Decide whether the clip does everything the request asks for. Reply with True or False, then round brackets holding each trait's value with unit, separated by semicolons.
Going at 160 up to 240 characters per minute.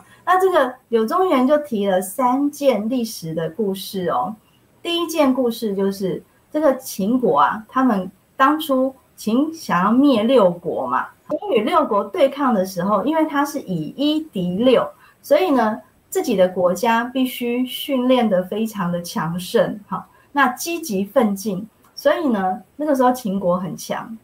True (230 characters per minute)